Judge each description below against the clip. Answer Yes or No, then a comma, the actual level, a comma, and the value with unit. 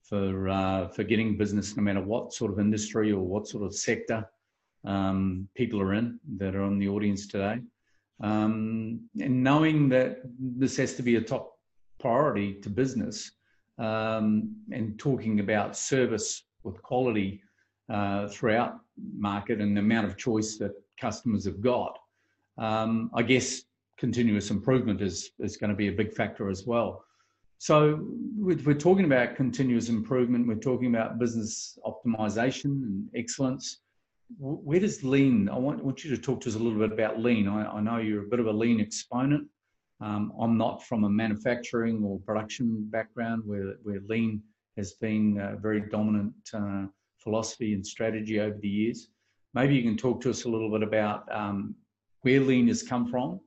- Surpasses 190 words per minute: No, average, 170 wpm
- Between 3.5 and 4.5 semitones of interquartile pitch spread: No, average, 2.9 semitones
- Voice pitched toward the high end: No, low, 110 Hz